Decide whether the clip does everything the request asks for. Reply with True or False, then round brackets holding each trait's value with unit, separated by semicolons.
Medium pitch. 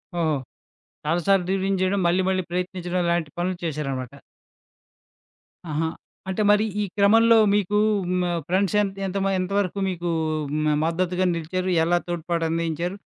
True (180 Hz)